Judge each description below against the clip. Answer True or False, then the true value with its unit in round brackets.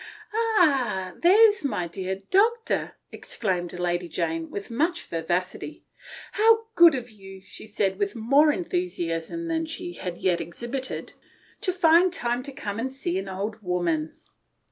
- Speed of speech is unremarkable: True (160 wpm)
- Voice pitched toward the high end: True (225 Hz)